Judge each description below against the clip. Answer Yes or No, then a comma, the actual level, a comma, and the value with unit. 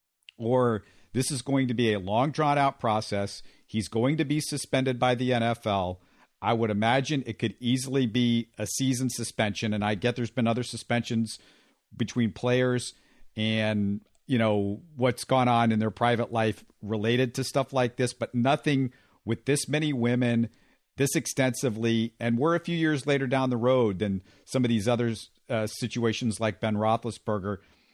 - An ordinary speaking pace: Yes, average, 170 wpm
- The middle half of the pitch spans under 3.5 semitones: Yes, average, 3.0 semitones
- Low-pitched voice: Yes, low, 120 Hz